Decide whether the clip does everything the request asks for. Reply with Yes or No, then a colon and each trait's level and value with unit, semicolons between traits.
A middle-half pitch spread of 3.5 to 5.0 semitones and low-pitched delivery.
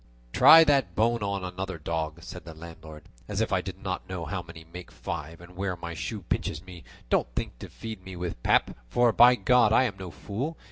Yes: average, 4.6 semitones; very low, 90 Hz